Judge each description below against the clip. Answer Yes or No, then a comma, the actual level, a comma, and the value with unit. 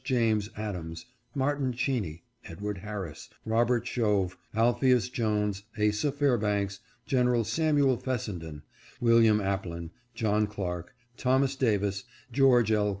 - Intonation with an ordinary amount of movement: Yes, average, 4.0 semitones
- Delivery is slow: Yes, slow, 105 wpm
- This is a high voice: No, low, 110 Hz